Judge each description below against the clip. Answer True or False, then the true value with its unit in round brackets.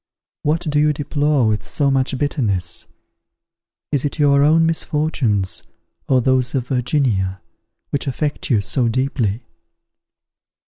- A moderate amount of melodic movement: True (4.0 semitones)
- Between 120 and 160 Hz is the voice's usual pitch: True (135 Hz)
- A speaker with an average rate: False (125 wpm)